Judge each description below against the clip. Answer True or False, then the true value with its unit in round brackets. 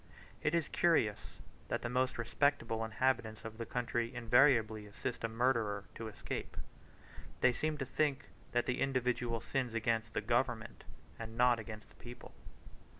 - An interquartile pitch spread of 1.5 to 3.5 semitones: True (2.5 semitones)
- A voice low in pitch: True (120 Hz)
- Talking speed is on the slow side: False (150 wpm)